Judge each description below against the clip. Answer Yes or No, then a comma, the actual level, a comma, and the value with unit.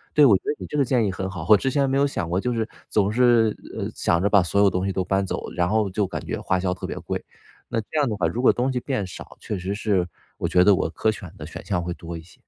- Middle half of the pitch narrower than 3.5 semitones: No, average, 4.6 semitones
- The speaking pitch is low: Yes, low, 100 Hz